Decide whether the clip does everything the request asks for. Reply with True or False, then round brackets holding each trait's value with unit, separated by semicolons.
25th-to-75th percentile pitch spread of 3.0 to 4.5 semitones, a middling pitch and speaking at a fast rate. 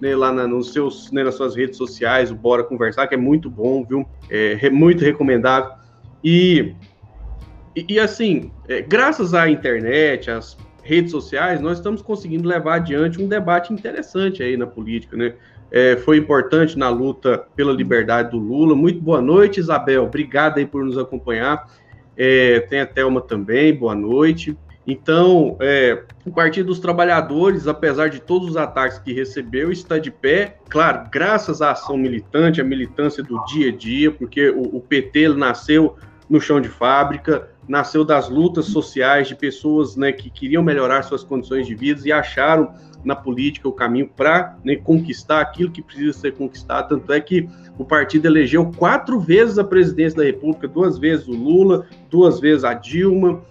False (4.1 semitones; 145 Hz; 175 wpm)